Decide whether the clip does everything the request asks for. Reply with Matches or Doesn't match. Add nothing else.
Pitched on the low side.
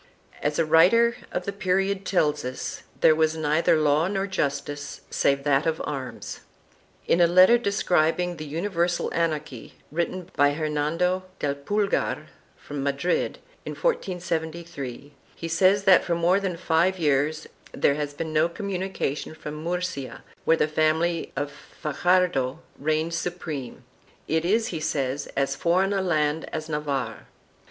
Doesn't match